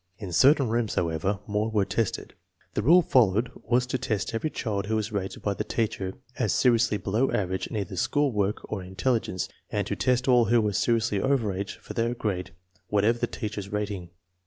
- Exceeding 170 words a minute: Yes, fast, 205 wpm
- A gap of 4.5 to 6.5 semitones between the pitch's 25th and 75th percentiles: No, average, 3.3 semitones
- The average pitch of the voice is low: Yes, low, 110 Hz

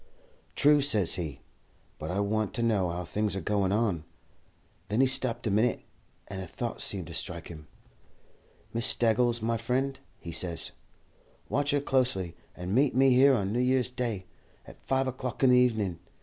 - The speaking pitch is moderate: No, low, 110 Hz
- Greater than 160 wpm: Yes, average, 180 wpm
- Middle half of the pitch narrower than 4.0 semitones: No, average, 5.2 semitones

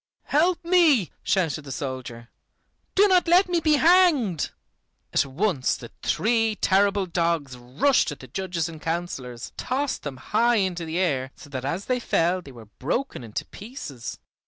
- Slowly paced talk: No, average, 160 wpm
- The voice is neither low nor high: Yes, medium, 180 Hz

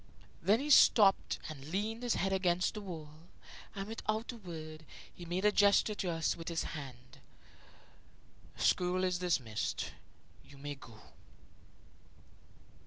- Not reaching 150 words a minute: Yes, slow, 135 wpm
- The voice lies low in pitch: No, medium, 180 Hz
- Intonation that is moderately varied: Yes, average, 4.6 semitones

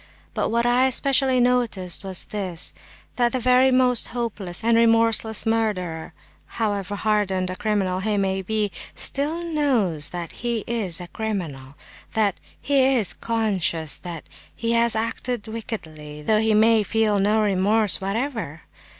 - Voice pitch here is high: Yes, high, 215 Hz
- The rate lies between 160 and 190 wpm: No, average, 140 wpm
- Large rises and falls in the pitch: No, average, 3.8 semitones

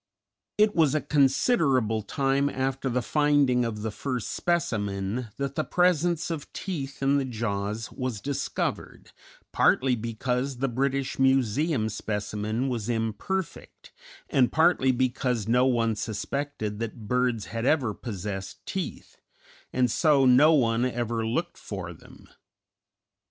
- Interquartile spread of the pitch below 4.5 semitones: Yes, average, 3.8 semitones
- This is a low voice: Yes, low, 125 Hz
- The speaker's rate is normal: No, slow, 130 wpm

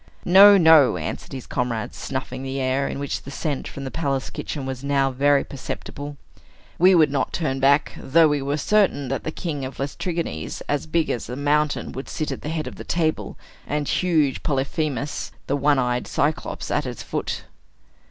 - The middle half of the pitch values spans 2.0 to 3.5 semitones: Yes, average, 2.7 semitones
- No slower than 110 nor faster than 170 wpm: No, average, 190 wpm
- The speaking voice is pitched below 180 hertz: Yes, medium, 140 Hz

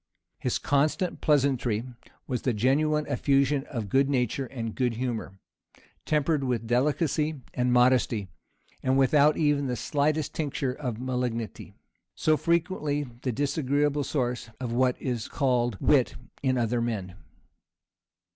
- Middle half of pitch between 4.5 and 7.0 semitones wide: No, average, 3.2 semitones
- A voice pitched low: Yes, low, 130 Hz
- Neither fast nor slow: No, slow, 125 wpm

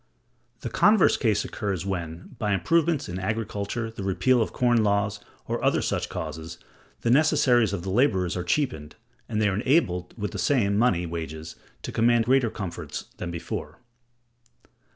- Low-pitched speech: Yes, low, 105 Hz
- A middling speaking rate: Yes, average, 160 wpm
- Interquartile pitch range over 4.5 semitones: Yes, average, 5.2 semitones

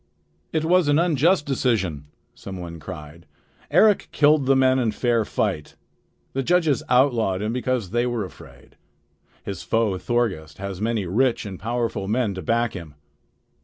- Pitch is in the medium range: No, low, 115 Hz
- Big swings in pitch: Yes, wide, 5.8 semitones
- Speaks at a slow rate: No, average, 155 wpm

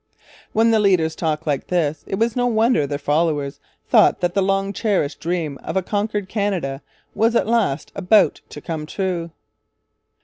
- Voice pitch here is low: No, medium, 185 Hz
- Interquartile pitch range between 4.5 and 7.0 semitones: Yes, average, 5.1 semitones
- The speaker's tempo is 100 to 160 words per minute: No, average, 170 wpm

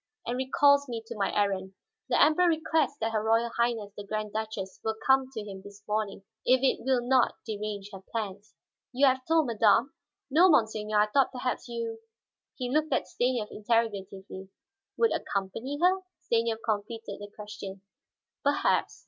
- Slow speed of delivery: No, average, 165 wpm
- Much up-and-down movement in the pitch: No, average, 4.0 semitones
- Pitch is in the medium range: No, high, 225 Hz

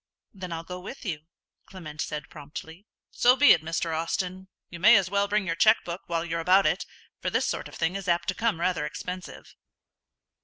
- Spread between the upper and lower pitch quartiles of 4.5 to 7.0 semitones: No, average, 2.9 semitones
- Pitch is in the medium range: Yes, medium, 180 Hz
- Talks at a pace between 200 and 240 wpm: Yes, fast, 205 wpm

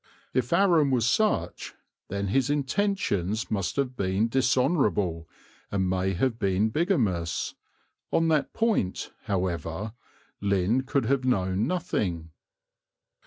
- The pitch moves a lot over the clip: Yes, wide, 6.7 semitones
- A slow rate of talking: Yes, slow, 115 wpm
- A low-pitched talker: Yes, low, 110 Hz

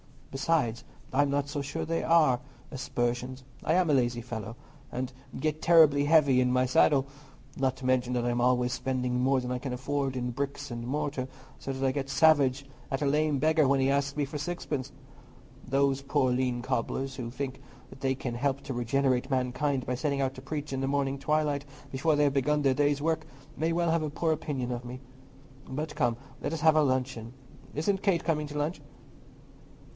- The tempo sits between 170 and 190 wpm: No, average, 200 wpm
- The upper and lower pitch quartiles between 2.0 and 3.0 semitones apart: Yes, narrow, 2.6 semitones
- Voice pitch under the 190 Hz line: Yes, low, 135 Hz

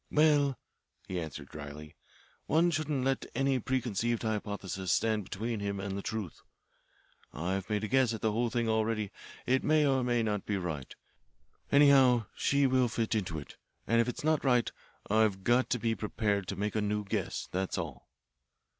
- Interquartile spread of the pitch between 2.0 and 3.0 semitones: No, average, 4.5 semitones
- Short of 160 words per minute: No, average, 180 wpm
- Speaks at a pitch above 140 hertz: No, low, 110 Hz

